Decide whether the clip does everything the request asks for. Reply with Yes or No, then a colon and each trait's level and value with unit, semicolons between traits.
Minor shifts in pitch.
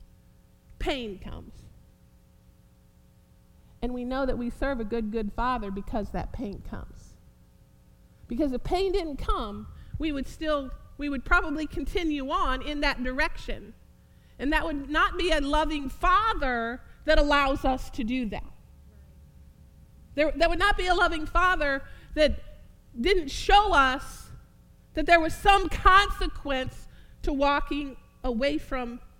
No: average, 4.8 semitones